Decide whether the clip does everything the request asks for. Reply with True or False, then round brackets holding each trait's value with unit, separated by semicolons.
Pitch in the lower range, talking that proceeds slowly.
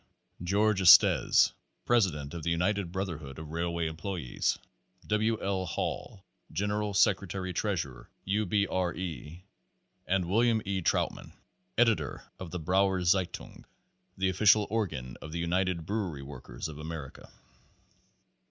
True (90 Hz; 125 wpm)